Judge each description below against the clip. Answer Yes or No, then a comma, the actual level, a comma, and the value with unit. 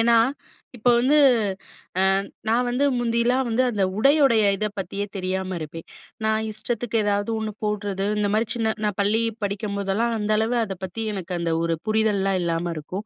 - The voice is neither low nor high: No, high, 210 Hz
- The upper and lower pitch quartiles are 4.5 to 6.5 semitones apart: No, average, 3.1 semitones